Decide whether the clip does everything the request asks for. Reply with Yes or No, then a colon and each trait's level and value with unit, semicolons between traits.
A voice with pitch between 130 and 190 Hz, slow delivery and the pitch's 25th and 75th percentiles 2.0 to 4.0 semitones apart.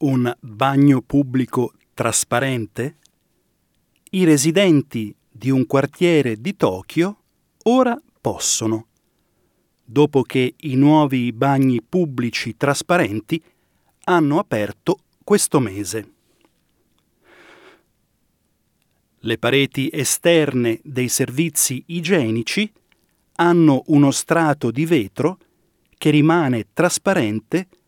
No: medium, 140 Hz; slow, 80 wpm; average, 5.1 semitones